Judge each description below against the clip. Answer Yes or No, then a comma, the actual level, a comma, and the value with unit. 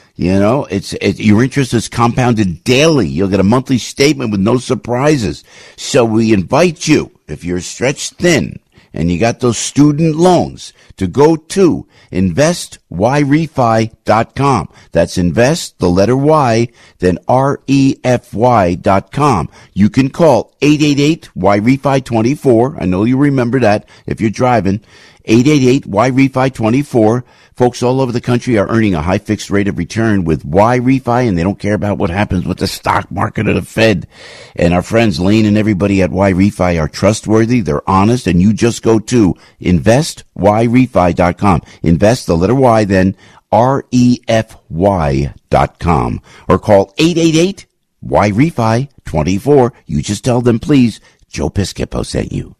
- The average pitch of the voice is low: Yes, low, 115 Hz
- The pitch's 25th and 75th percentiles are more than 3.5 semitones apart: Yes, average, 5.0 semitones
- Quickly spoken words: No, average, 165 wpm